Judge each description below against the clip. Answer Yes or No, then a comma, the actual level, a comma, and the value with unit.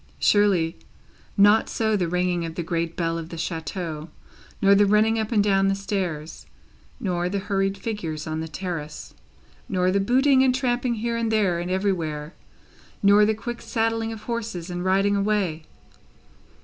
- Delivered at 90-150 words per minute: No, average, 165 wpm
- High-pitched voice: Yes, high, 195 Hz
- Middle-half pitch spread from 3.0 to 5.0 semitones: Yes, average, 4.2 semitones